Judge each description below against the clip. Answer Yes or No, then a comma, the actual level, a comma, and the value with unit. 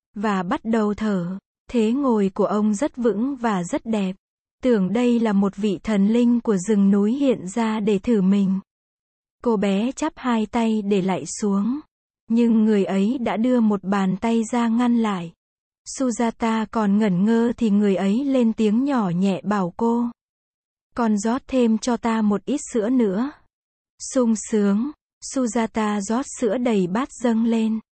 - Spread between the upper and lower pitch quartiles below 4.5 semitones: Yes, average, 2.8 semitones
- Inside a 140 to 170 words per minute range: Yes, slow, 165 wpm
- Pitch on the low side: No, high, 225 Hz